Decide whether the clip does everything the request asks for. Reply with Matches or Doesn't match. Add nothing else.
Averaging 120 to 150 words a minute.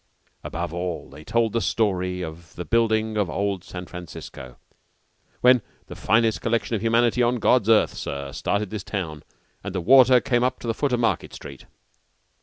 Doesn't match